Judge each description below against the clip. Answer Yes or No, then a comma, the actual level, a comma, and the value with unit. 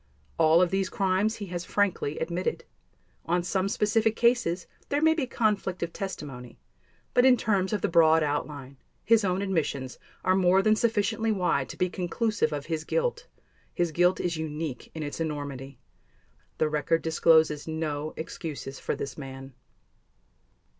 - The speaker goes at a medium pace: Yes, average, 155 wpm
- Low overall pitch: No, medium, 175 Hz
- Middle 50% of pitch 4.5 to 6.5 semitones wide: Yes, average, 5.0 semitones